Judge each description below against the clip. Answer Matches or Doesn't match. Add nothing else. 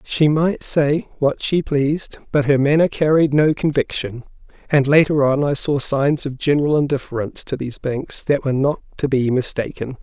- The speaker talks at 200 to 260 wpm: Doesn't match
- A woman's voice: Doesn't match